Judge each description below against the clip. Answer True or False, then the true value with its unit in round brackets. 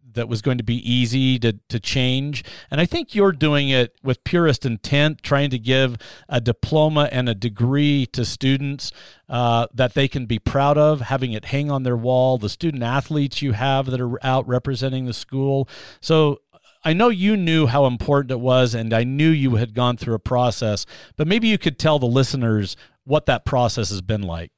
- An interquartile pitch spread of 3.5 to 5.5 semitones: False (3.0 semitones)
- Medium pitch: False (130 Hz)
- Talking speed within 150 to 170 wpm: False (205 wpm)